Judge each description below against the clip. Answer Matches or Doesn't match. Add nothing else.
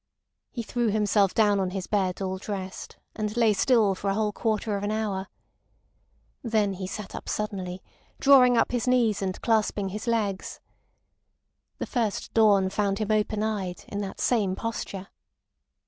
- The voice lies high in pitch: Matches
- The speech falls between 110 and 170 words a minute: Matches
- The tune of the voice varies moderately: Doesn't match